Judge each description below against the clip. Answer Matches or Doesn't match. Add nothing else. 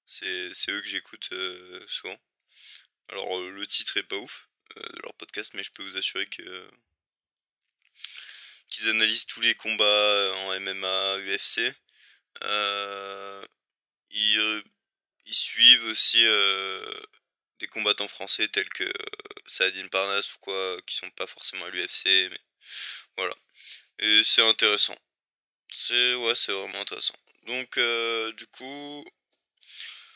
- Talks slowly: Matches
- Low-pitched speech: Matches